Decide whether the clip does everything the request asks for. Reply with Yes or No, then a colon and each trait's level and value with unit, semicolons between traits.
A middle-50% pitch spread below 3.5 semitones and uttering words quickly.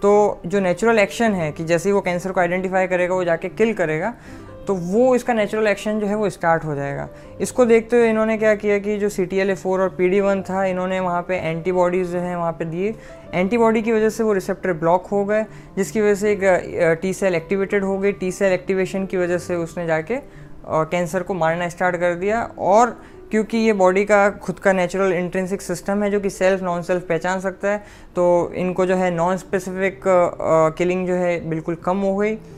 Yes: narrow, 2.5 semitones; fast, 210 wpm